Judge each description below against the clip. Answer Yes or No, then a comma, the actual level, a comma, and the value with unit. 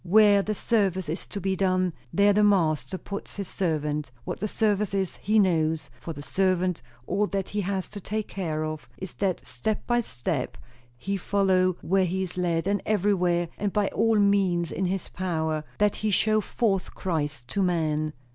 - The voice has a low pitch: No, high, 190 Hz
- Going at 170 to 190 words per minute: Yes, average, 185 wpm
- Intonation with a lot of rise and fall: No, average, 3.3 semitones